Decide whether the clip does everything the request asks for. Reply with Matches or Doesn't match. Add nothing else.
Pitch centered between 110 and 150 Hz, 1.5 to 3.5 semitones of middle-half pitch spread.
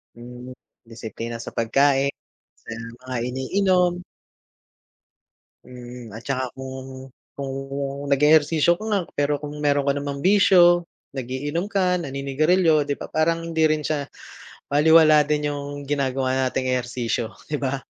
Matches